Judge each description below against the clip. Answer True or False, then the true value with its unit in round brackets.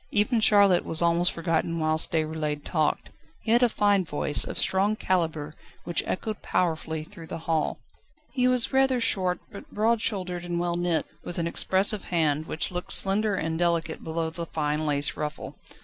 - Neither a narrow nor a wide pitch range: True (4.1 semitones)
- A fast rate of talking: False (175 wpm)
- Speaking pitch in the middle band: True (175 Hz)